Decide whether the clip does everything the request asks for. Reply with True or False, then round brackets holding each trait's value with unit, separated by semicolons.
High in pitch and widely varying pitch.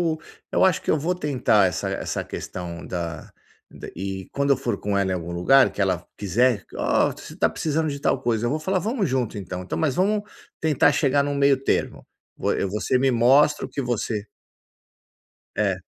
False (130 Hz; 6.8 semitones)